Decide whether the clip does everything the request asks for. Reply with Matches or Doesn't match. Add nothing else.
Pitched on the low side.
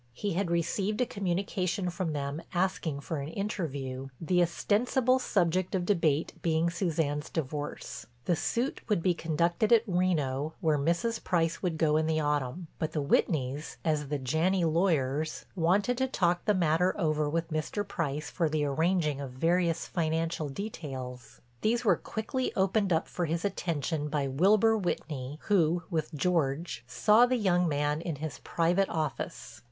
Doesn't match